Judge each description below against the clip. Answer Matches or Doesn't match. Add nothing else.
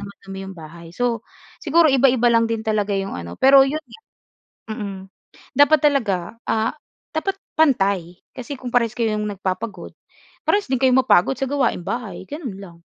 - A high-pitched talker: Matches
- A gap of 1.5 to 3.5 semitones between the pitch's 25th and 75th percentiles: Doesn't match